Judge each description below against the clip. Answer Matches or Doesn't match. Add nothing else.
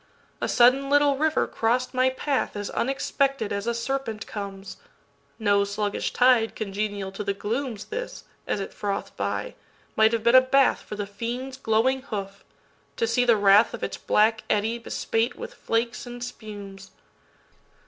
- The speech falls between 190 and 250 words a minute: Doesn't match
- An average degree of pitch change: Matches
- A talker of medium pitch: Doesn't match